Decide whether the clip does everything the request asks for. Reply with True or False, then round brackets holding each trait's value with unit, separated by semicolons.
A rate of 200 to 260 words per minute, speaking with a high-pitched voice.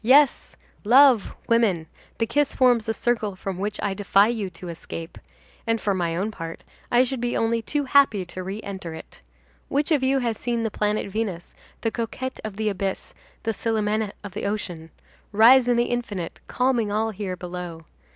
False (185 wpm; 215 Hz)